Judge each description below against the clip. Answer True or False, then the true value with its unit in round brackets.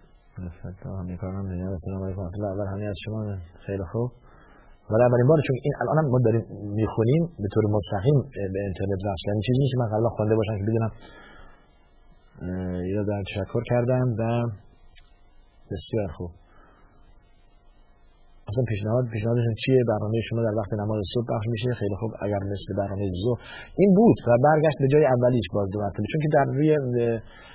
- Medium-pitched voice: False (110 Hz)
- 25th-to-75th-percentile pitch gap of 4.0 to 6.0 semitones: False (3.5 semitones)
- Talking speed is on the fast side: True (165 wpm)